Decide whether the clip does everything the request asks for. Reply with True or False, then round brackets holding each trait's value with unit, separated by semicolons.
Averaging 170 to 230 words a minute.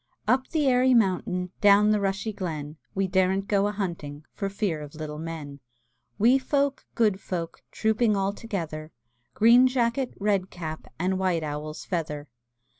False (155 wpm)